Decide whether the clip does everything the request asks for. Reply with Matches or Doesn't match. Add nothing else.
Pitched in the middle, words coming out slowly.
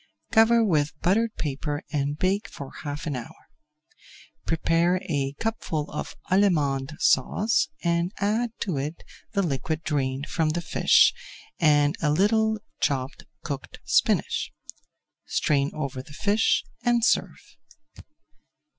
Matches